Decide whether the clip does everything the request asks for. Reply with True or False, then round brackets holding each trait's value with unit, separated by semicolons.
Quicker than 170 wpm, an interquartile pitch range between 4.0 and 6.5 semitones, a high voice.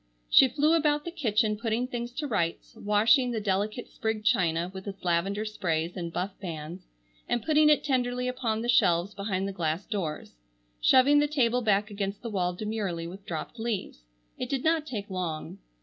True (180 wpm; 5.1 semitones; 215 Hz)